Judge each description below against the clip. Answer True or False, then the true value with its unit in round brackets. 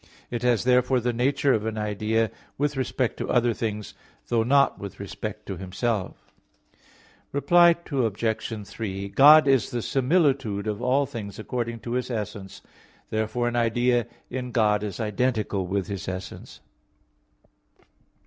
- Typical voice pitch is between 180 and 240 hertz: False (115 Hz)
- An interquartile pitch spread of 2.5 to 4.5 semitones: True (3.2 semitones)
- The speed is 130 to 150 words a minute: True (140 wpm)